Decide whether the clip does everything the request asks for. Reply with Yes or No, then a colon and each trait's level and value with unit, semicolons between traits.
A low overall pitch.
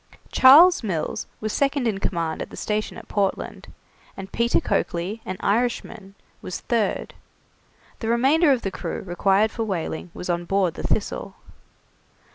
No: high, 210 Hz